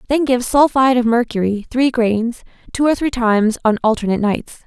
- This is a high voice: Yes, high, 240 Hz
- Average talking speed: Yes, average, 180 wpm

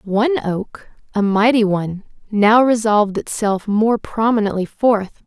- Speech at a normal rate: No, slow, 125 wpm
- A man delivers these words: No, female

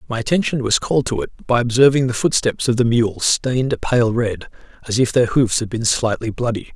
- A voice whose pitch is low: Yes, low, 120 Hz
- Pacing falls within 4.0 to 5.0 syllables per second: No, 5.5 syllables/s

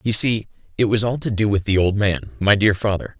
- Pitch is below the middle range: Yes, low, 105 Hz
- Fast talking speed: Yes, fast, 265 wpm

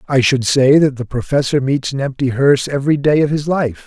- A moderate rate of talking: No, fast, 235 wpm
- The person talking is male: Yes, male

